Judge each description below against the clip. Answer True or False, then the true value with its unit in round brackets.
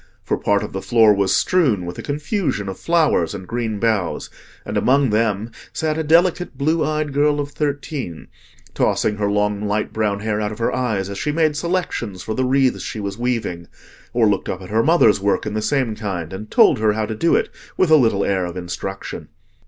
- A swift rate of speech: True (215 wpm)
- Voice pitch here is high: False (110 Hz)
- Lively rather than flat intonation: True (6.3 semitones)